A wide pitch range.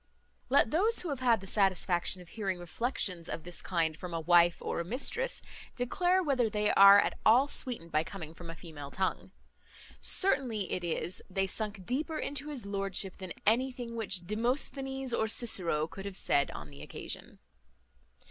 Yes: wide, 6.3 semitones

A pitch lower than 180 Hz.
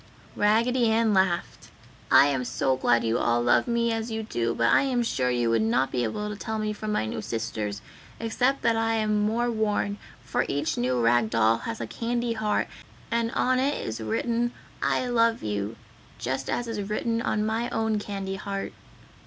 No: high, 210 Hz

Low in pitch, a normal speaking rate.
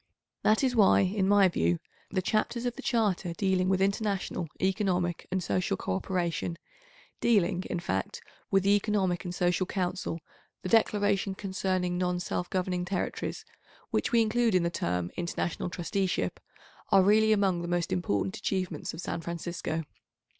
No: medium, 185 Hz; average, 155 wpm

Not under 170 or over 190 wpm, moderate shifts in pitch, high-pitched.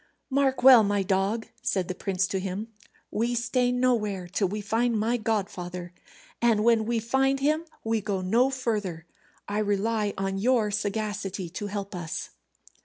No: average, 160 wpm; average, 3.5 semitones; high, 210 Hz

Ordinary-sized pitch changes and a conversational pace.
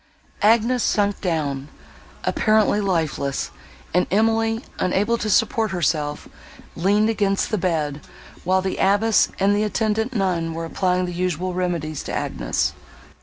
No: average, 4.4 semitones; slow, 130 wpm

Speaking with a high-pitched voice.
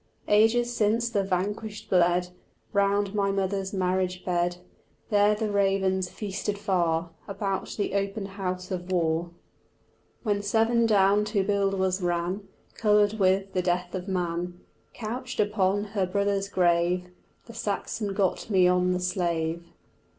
Yes: high, 195 Hz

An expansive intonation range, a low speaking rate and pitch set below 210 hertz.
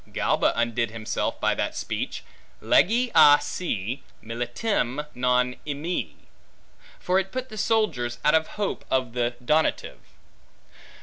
Yes: wide, 7.9 semitones; slow, 125 wpm; medium, 140 Hz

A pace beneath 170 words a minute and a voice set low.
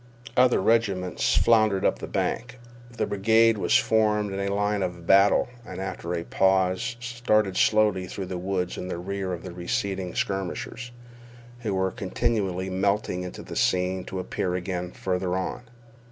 Yes: average, 155 wpm; very low, 95 Hz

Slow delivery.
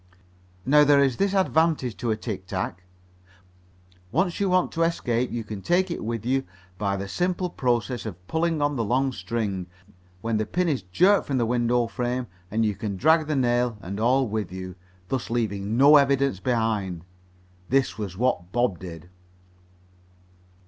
No: average, 170 wpm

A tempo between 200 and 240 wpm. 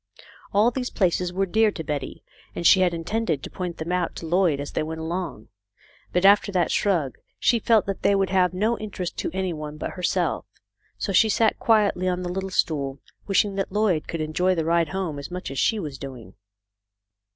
Yes: fast, 205 wpm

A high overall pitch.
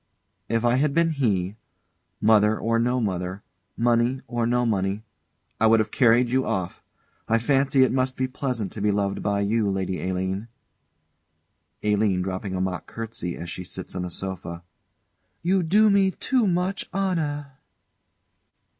No: low, 115 Hz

